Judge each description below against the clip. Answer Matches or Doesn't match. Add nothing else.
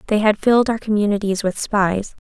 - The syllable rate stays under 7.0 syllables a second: Matches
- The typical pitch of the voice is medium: Doesn't match